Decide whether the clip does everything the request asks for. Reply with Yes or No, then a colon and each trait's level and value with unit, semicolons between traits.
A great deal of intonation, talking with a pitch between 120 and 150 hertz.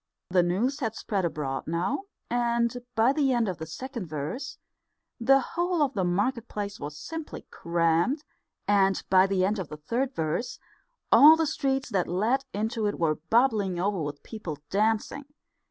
No: wide, 6.8 semitones; high, 210 Hz